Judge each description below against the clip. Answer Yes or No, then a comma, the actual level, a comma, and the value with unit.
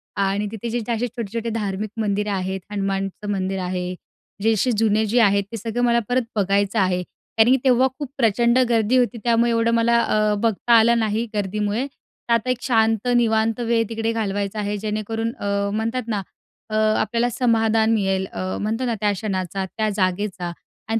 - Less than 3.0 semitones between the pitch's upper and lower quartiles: Yes, narrow, 2.4 semitones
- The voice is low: No, high, 220 Hz